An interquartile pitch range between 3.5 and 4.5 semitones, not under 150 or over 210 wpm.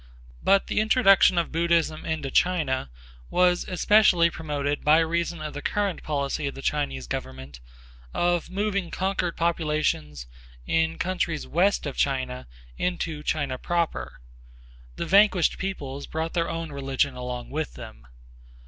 No: average, 4.0 semitones; slow, 135 wpm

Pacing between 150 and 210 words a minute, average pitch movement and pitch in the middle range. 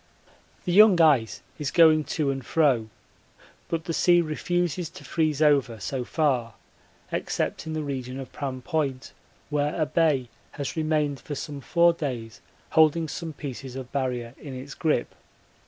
Yes: average, 155 wpm; average, 3.4 semitones; medium, 145 Hz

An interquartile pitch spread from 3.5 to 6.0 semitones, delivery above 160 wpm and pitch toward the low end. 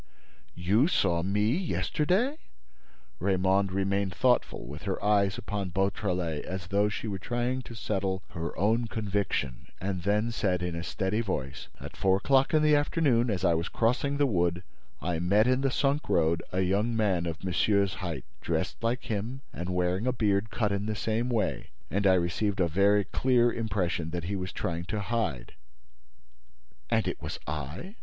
Yes: average, 4.3 semitones; average, 175 wpm; low, 100 Hz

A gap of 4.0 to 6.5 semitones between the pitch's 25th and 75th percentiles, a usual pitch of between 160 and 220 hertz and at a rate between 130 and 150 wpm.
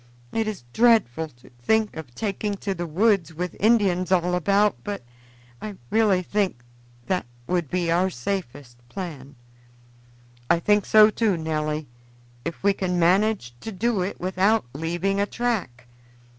Yes: average, 4.3 semitones; medium, 185 Hz; average, 145 wpm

